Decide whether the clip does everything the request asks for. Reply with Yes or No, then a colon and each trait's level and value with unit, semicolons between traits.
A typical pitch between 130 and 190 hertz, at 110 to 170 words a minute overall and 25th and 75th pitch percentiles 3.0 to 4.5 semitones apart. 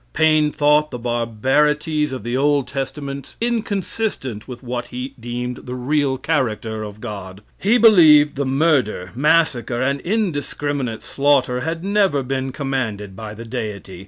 Yes: low, 135 Hz; average, 140 wpm; average, 4.0 semitones